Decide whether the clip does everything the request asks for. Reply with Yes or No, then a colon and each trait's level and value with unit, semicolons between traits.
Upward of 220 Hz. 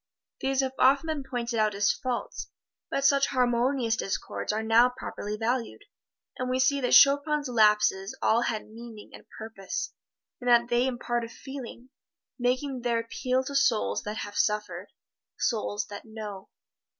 Yes: high, 240 Hz